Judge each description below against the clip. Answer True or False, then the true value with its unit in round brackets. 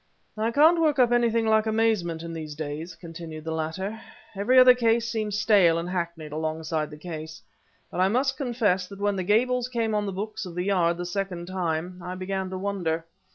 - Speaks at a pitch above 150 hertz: True (190 Hz)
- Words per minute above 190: True (200 wpm)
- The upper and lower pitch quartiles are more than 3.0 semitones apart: True (4.9 semitones)